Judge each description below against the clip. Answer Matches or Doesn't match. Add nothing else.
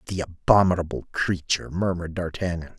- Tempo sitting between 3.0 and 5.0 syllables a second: Doesn't match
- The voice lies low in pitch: Matches